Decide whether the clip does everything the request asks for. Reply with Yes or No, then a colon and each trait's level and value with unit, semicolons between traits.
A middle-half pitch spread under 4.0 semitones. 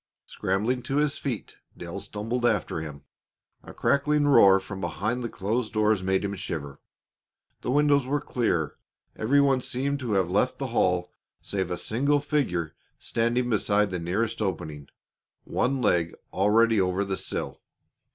No: average, 5.3 semitones